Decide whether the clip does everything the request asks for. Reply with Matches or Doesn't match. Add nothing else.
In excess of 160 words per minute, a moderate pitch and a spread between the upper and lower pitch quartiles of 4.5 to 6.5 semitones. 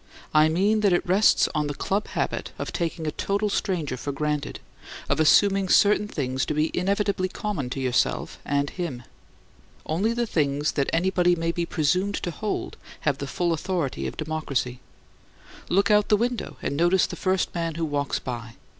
Matches